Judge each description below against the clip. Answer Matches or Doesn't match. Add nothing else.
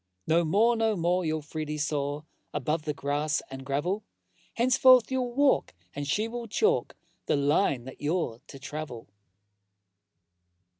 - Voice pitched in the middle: Matches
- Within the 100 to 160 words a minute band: Matches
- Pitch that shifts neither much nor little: Doesn't match